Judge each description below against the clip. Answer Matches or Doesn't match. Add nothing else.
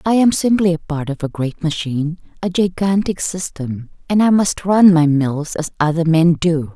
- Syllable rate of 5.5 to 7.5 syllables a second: Doesn't match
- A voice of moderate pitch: Matches